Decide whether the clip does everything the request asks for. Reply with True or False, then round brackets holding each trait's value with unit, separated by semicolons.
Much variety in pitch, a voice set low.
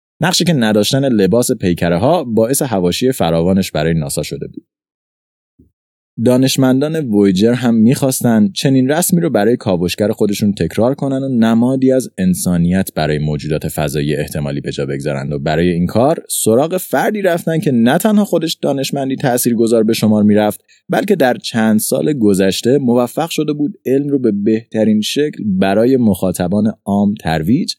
True (7.0 semitones; 110 Hz)